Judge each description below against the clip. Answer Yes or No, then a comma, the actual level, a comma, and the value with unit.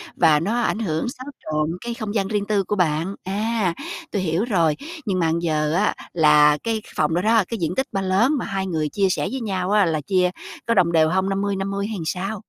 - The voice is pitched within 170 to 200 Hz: Yes, high, 190 Hz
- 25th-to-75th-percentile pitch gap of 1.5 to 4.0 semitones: No, average, 4.4 semitones